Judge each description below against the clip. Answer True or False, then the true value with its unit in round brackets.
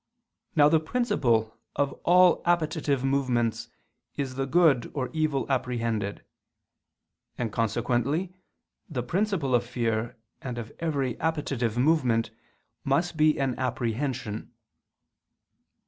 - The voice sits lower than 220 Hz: True (135 Hz)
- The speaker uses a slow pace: True (105 wpm)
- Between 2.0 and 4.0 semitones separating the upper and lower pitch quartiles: False (4.7 semitones)